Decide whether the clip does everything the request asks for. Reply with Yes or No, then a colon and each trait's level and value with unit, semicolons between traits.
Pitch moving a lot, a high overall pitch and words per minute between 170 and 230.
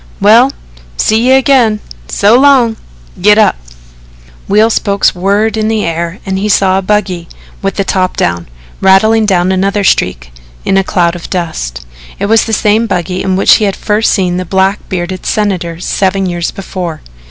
No: average, 2.9 semitones; high, 195 Hz; average, 175 wpm